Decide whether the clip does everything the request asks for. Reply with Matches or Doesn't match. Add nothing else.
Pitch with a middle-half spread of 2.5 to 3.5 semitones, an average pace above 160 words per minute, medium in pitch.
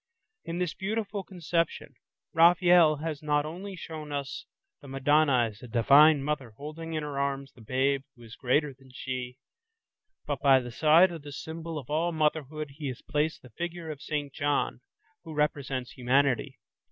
Matches